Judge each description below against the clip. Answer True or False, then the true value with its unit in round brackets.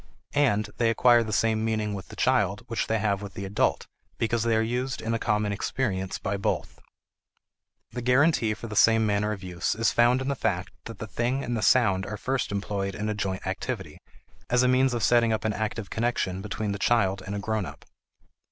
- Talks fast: True (215 wpm)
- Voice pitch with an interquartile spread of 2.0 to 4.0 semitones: True (2.8 semitones)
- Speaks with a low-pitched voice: True (110 Hz)